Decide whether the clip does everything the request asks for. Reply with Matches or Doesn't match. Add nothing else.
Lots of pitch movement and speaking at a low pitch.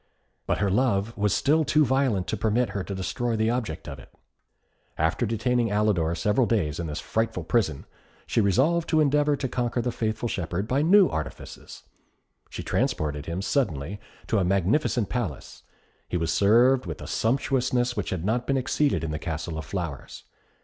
Matches